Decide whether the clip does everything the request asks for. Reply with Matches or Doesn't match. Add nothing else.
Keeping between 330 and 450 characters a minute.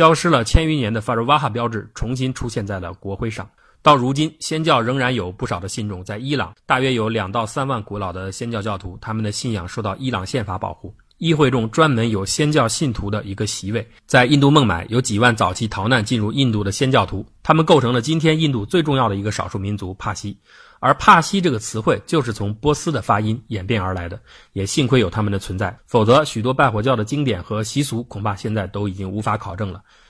Matches